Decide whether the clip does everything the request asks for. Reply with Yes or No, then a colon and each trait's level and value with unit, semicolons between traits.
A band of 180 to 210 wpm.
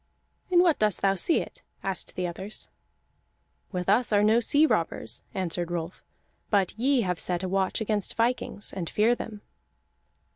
No: average, 160 wpm